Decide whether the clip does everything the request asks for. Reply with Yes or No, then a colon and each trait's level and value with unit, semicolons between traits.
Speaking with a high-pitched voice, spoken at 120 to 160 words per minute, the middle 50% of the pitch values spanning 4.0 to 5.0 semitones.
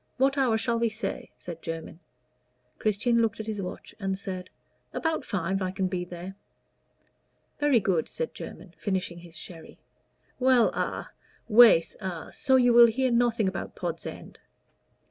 Yes: high, 215 Hz; average, 155 wpm; average, 4.6 semitones